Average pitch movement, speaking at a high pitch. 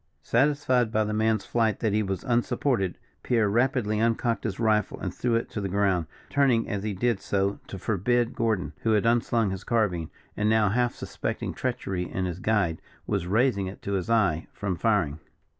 No: average, 3.2 semitones; low, 110 Hz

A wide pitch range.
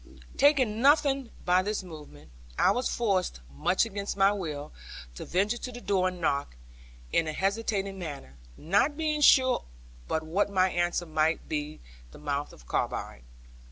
Yes: wide, 6.5 semitones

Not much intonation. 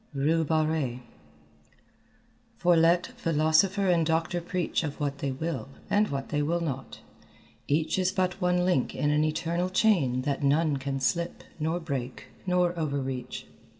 No: average, 3.8 semitones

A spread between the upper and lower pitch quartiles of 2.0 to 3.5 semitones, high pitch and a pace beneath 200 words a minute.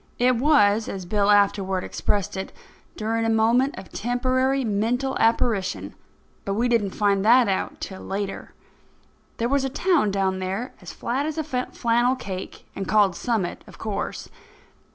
No: average, 4.1 semitones; high, 220 Hz; average, 155 wpm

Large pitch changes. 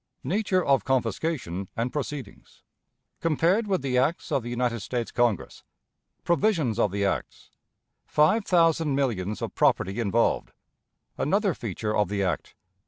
Yes: wide, 7.5 semitones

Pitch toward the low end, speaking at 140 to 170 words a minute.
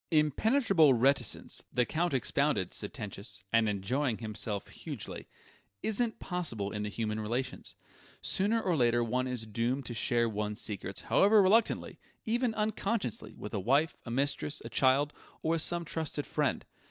Yes: low, 130 Hz; average, 150 wpm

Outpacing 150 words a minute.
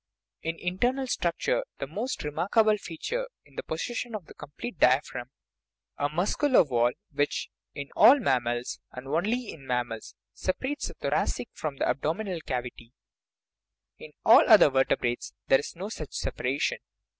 No: average, 145 wpm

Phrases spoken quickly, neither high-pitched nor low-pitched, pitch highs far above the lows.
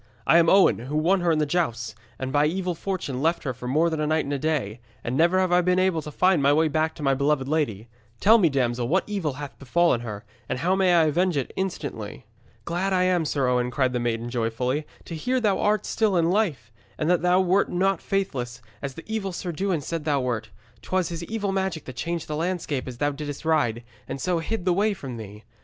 Yes: fast, 240 wpm; medium, 155 Hz; wide, 5.7 semitones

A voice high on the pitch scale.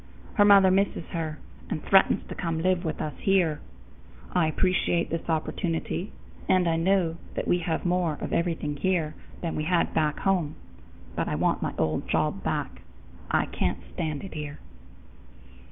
No: medium, 170 Hz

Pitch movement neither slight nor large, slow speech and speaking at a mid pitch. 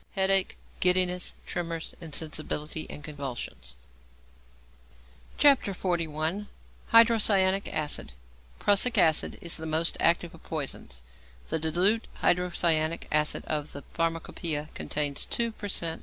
Yes: average, 3.5 semitones; slow, 105 wpm; medium, 165 Hz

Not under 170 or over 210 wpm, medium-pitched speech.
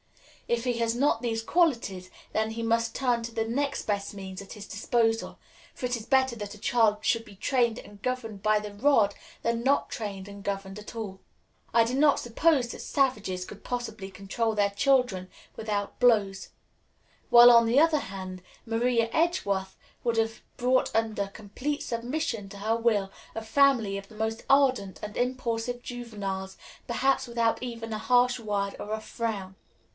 No: average, 175 wpm; high, 225 Hz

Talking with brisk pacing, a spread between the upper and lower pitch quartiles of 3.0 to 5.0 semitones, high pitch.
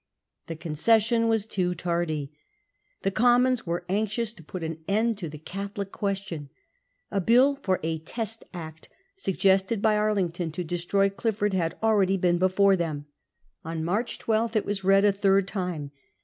No: average, 165 wpm; average, 3.8 semitones; high, 195 Hz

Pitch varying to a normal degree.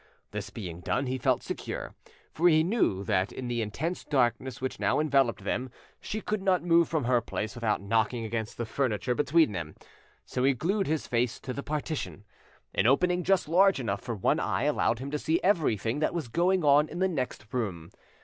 No: wide, 6.2 semitones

